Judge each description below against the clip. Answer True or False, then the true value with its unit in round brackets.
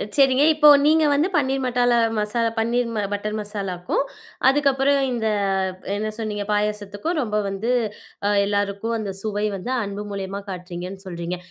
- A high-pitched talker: True (210 Hz)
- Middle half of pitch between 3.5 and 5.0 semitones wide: True (3.9 semitones)